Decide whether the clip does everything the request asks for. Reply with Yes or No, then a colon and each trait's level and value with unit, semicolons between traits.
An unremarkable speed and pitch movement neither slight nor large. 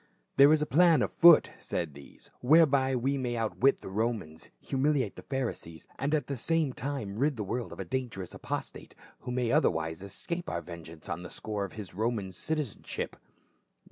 No: average, 195 wpm; wide, 6.4 semitones